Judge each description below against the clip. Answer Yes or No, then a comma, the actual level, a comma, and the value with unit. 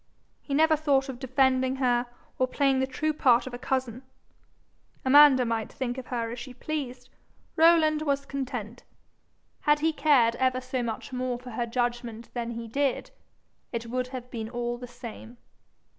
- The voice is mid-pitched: No, very high, 255 Hz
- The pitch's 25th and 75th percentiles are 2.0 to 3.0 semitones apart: Yes, narrow, 2.4 semitones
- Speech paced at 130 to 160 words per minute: No, average, 170 wpm